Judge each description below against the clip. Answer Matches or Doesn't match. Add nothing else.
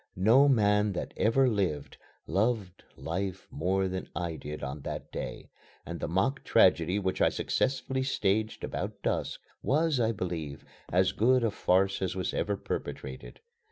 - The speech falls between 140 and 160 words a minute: Matches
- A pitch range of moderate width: Matches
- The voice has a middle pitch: Doesn't match